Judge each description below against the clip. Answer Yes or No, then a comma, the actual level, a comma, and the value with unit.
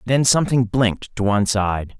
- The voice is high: No, low, 110 Hz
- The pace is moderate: Yes, average, 180 wpm